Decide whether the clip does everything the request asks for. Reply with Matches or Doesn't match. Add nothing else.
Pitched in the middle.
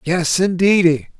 Matches